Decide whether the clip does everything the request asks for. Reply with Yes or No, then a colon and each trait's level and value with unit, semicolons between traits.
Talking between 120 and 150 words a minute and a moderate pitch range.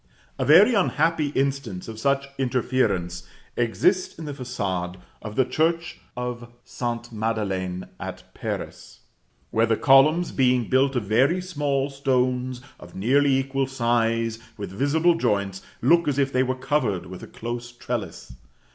Yes: average, 145 wpm; average, 3.6 semitones